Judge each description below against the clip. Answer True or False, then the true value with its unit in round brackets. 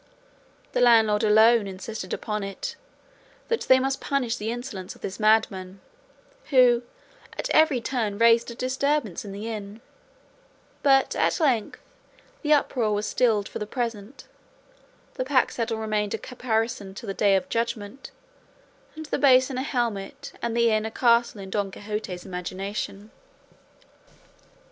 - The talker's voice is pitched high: True (225 Hz)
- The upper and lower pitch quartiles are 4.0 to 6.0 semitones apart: False (3.5 semitones)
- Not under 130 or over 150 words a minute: True (145 wpm)